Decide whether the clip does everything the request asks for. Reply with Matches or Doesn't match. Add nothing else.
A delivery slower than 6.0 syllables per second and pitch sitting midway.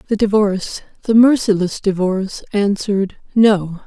Doesn't match